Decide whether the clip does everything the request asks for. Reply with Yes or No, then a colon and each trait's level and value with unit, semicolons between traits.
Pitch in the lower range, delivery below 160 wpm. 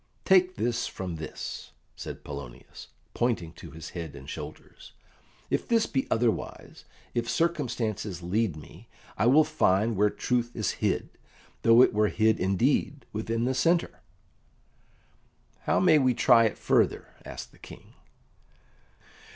Yes: low, 115 Hz; slow, 135 wpm